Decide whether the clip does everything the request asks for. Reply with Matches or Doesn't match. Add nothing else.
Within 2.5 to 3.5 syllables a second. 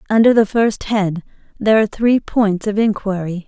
Doesn't match